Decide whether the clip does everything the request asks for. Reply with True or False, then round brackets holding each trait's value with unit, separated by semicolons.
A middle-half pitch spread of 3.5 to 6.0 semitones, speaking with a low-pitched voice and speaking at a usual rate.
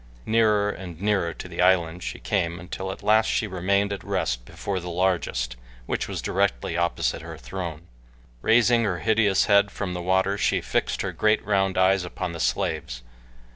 False (2.8 semitones; 95 Hz; 175 wpm)